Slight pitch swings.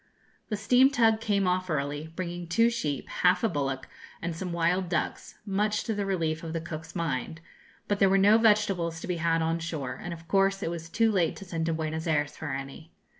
No: average, 3.7 semitones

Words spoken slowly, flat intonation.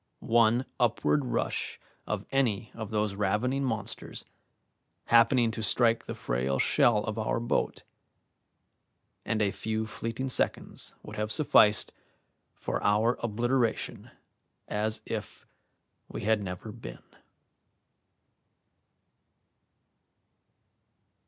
Yes: slow, 100 wpm; narrow, 2.1 semitones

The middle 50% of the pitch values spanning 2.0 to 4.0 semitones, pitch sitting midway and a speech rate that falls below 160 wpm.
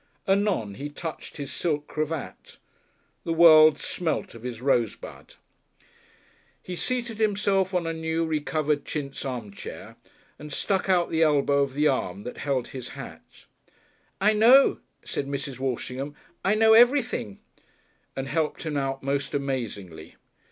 No: average, 4.7 semitones; medium, 150 Hz; average, 140 wpm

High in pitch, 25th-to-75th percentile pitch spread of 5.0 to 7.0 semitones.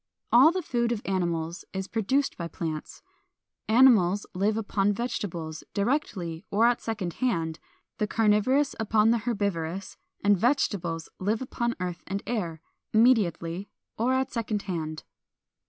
Yes: high, 205 Hz; wide, 5.4 semitones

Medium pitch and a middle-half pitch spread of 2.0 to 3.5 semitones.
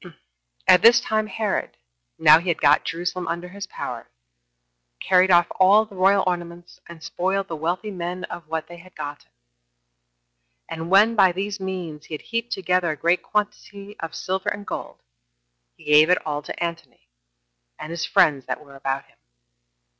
Yes: medium, 180 Hz; average, 3.1 semitones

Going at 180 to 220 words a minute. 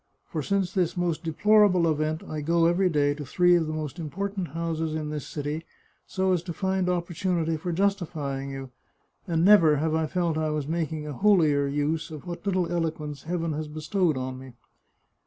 Yes: average, 190 wpm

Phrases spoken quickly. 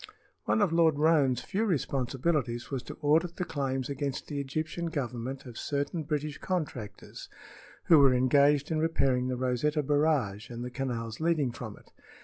No: average, 160 wpm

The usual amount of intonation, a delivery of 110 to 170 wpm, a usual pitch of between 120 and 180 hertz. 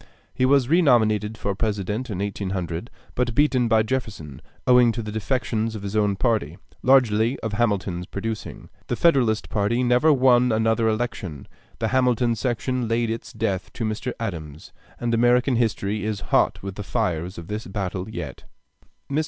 No: average, 3.3 semitones; average, 165 wpm; low, 110 Hz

